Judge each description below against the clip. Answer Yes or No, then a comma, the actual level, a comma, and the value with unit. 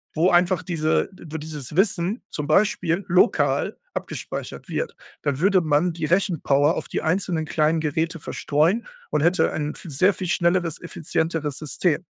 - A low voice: No, medium, 165 Hz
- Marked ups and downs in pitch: No, average, 2.9 semitones